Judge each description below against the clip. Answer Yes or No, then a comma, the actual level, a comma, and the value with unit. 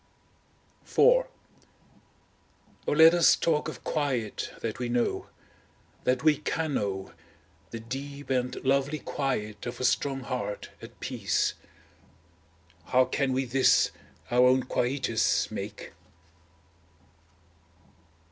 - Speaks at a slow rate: Yes, slow, 110 wpm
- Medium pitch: No, low, 130 Hz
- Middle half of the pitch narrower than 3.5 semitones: Yes, average, 2.9 semitones